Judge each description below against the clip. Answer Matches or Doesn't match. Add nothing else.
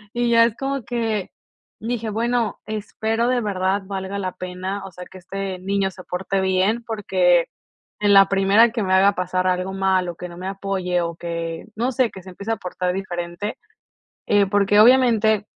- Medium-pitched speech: Doesn't match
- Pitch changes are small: Doesn't match